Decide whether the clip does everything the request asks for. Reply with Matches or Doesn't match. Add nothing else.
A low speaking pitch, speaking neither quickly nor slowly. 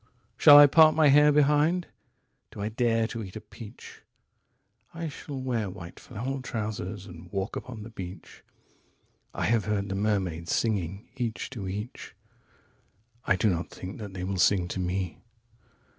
Matches